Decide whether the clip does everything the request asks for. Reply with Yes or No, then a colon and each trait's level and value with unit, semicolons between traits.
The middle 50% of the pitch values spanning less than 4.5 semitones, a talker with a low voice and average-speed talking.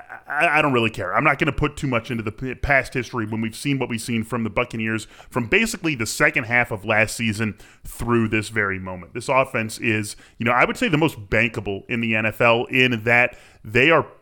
No: average, 2.7 semitones; low, 115 Hz; fast, 230 wpm